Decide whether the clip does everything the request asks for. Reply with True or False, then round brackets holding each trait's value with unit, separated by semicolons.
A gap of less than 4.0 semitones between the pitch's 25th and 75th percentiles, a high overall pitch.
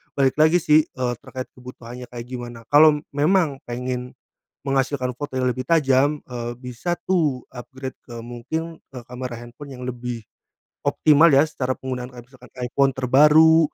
False (2.9 semitones; 130 Hz)